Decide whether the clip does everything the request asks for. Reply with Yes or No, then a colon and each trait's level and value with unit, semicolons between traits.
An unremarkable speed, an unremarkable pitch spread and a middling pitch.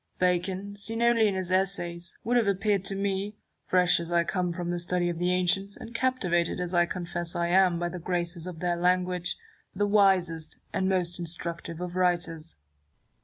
No: average, 185 wpm; narrow, 2.0 semitones; medium, 180 Hz